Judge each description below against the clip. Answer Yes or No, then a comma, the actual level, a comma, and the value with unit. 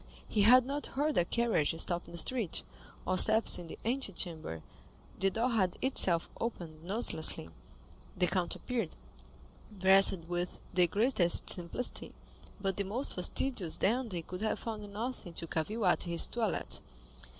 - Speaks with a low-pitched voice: No, high, 195 Hz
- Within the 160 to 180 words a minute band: No, average, 150 wpm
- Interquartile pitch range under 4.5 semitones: No, average, 5.2 semitones